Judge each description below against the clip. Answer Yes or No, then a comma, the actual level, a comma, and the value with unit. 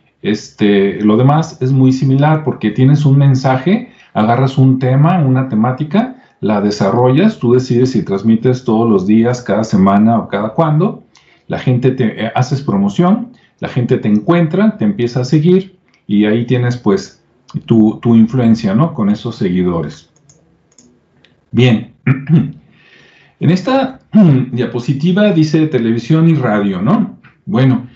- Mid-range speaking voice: No, low, 130 Hz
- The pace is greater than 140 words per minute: No, average, 135 wpm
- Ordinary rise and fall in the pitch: No, wide, 6.0 semitones